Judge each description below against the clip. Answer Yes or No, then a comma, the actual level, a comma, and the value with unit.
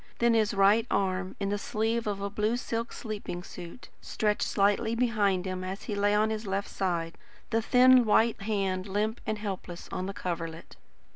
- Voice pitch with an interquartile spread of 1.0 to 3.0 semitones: Yes, average, 2.7 semitones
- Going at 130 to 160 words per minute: No, average, 185 wpm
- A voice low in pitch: No, high, 205 Hz